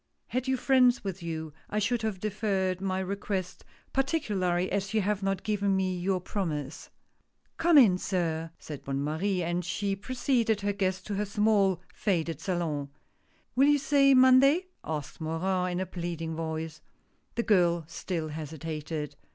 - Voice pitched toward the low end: No, high, 190 Hz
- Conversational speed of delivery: Yes, average, 170 wpm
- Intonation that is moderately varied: Yes, average, 4.3 semitones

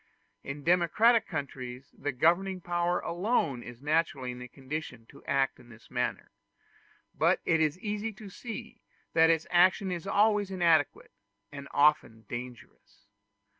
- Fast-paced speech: No, average, 140 wpm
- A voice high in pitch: No, medium, 160 Hz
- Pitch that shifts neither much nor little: No, wide, 5.9 semitones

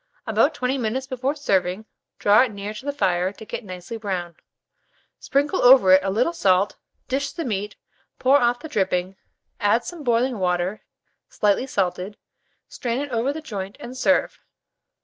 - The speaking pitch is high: Yes, high, 225 Hz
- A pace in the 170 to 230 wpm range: No, average, 160 wpm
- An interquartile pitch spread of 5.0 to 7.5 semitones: Yes, wide, 5.4 semitones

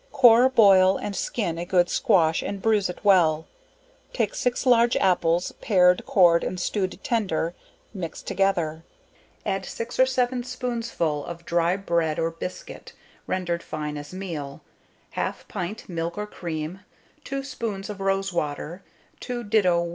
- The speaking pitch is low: No, medium, 185 Hz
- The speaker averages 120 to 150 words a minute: Yes, average, 145 wpm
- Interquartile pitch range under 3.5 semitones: No, average, 4.4 semitones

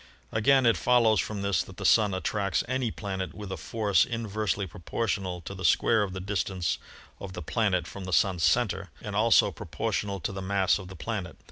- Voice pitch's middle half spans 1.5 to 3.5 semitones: Yes, narrow, 2.6 semitones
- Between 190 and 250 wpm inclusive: Yes, average, 200 wpm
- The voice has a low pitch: Yes, low, 100 Hz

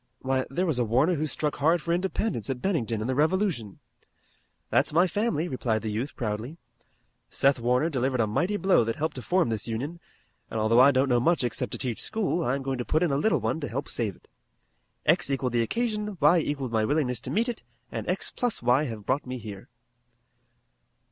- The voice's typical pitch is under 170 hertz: Yes, low, 135 Hz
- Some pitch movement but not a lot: No, wide, 6.0 semitones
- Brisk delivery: Yes, fast, 215 wpm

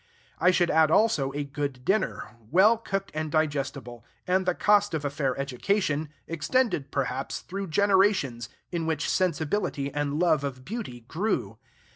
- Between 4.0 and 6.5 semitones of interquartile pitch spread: Yes, wide, 5.5 semitones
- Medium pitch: Yes, medium, 155 Hz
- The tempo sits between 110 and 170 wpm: Yes, average, 150 wpm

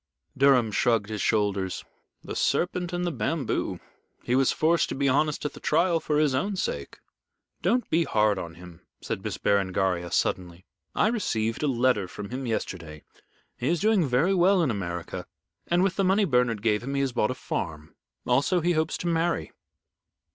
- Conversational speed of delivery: Yes, average, 185 wpm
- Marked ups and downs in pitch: Yes, wide, 8.6 semitones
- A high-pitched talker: No, low, 130 Hz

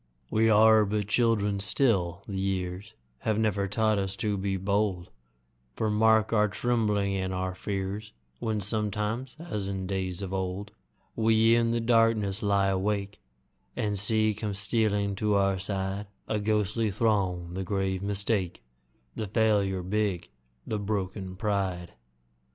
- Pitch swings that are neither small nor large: No, narrow, 2.1 semitones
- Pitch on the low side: Yes, low, 100 Hz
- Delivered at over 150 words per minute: No, average, 140 wpm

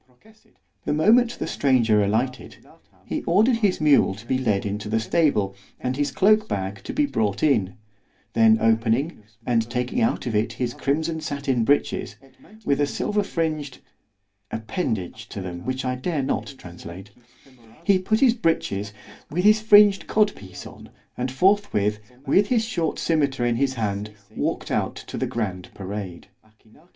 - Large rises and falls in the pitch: Yes, wide, 7.8 semitones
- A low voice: Yes, low, 130 Hz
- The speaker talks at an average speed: Yes, average, 155 wpm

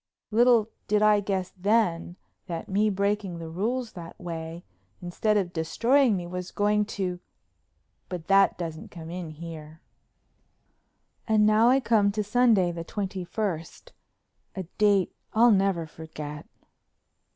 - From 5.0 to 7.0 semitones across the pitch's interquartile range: No, average, 3.9 semitones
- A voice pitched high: Yes, high, 195 Hz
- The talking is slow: Yes, slow, 130 wpm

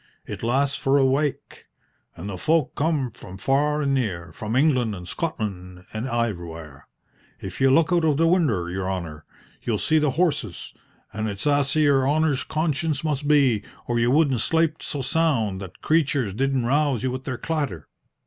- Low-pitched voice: Yes, low, 130 Hz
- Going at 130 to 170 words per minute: No, average, 180 wpm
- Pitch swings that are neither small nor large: No, wide, 6.4 semitones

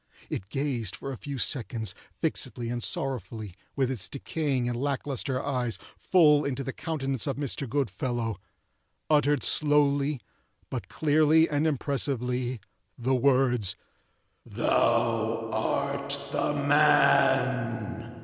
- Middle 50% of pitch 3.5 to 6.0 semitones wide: No, average, 3.1 semitones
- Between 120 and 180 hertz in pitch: Yes, low, 135 Hz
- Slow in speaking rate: Yes, slow, 110 wpm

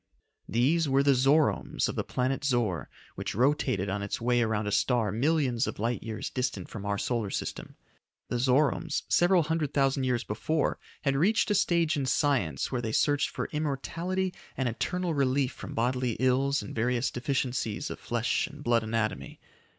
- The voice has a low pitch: Yes, low, 130 Hz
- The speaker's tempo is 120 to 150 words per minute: No, average, 175 wpm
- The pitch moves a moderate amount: Yes, average, 4.1 semitones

